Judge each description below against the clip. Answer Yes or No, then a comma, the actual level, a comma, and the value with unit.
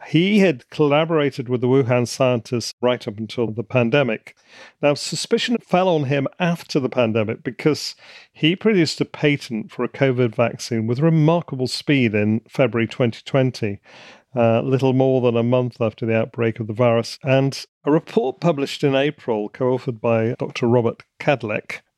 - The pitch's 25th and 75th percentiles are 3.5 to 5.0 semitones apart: Yes, average, 4.0 semitones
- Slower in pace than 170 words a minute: Yes, average, 160 wpm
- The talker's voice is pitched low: Yes, low, 130 Hz